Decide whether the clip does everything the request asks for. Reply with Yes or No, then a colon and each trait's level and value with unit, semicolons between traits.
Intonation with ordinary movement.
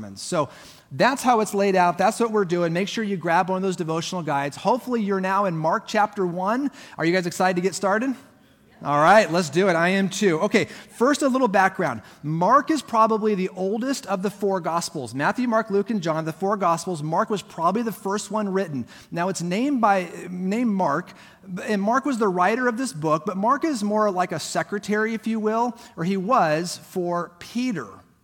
Yes: average, 4.1 semitones